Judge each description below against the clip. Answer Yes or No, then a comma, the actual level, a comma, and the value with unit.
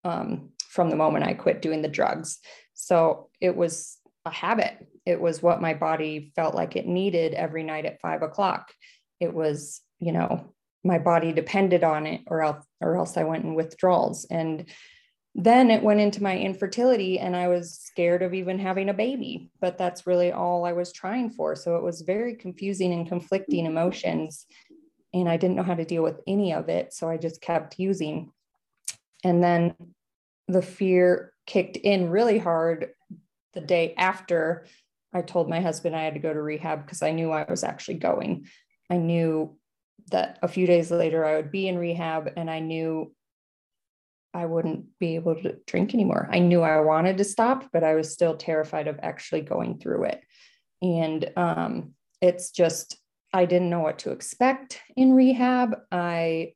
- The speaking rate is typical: Yes, average, 180 wpm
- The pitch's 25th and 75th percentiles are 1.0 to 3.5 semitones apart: Yes, average, 2.8 semitones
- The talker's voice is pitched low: No, medium, 175 Hz